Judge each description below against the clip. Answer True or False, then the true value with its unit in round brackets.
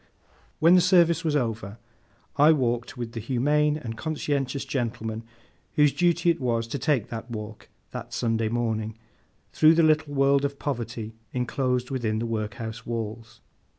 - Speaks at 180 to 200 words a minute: False (150 wpm)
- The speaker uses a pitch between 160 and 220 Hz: False (125 Hz)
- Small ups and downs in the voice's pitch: False (4.6 semitones)